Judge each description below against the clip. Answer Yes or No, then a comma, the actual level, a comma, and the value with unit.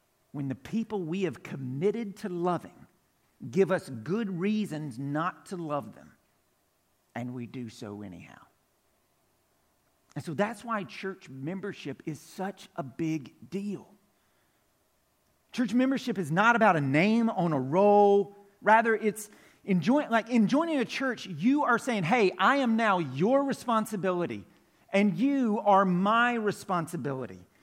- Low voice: No, high, 195 Hz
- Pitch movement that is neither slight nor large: No, wide, 5.8 semitones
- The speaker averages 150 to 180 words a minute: No, average, 140 wpm